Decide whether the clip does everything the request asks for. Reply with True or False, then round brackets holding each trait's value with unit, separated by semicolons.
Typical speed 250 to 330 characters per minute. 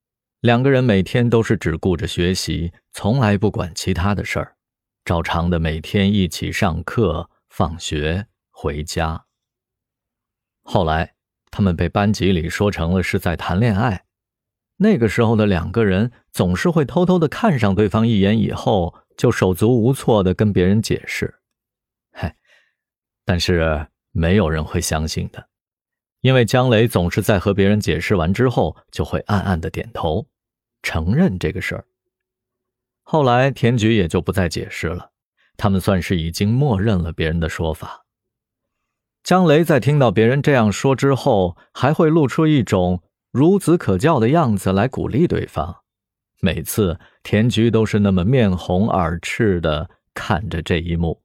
False (225 characters per minute)